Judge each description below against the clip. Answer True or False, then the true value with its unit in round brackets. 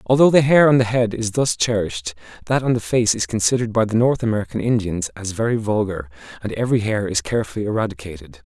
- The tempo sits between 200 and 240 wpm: True (205 wpm)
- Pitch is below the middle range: True (110 Hz)